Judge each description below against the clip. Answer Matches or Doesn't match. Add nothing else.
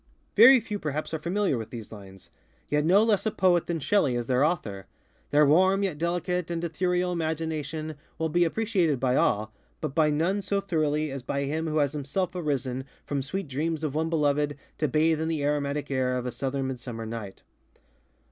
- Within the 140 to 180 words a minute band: Doesn't match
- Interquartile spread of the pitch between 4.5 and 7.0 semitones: Doesn't match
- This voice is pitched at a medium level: Matches